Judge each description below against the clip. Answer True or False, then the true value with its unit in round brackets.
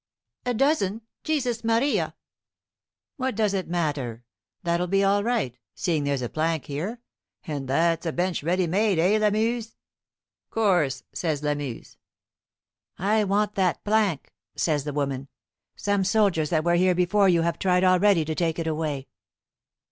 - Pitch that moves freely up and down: False (5.0 semitones)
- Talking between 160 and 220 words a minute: False (150 wpm)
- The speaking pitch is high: False (180 Hz)